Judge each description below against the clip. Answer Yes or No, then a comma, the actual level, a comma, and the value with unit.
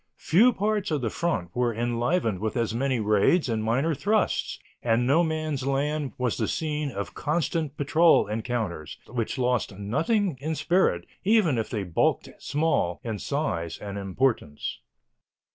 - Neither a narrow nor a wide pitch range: No, wide, 6.2 semitones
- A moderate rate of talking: Yes, average, 150 wpm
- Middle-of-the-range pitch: No, low, 130 Hz